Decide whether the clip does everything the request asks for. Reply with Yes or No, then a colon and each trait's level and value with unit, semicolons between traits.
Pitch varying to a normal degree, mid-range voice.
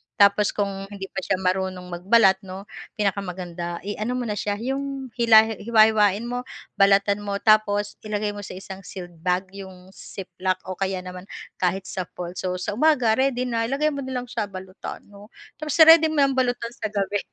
No: average, 3.7 semitones; high, 205 Hz